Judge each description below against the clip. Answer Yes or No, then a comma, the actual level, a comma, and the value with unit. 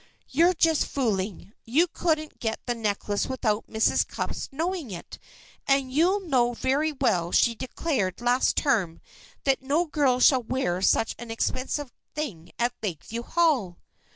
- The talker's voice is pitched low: No, very high, 255 Hz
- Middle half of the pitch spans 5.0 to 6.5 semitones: Yes, wide, 5.4 semitones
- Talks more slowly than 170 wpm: Yes, average, 145 wpm